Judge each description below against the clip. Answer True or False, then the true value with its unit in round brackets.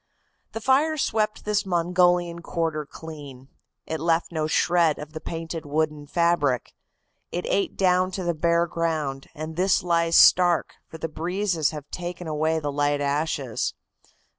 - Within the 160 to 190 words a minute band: False (150 wpm)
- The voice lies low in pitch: False (165 Hz)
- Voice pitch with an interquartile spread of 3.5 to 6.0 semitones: False (2.5 semitones)